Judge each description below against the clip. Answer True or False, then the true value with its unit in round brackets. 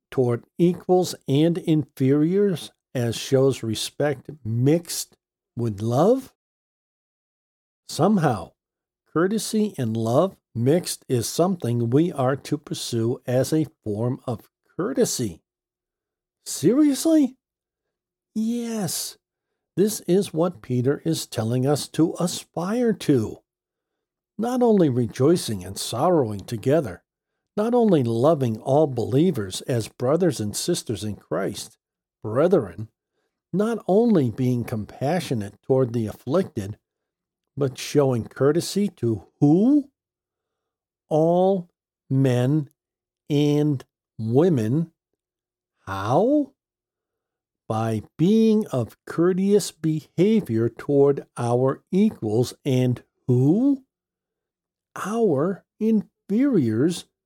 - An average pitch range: False (7.3 semitones)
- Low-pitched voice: False (150 Hz)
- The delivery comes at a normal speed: False (90 wpm)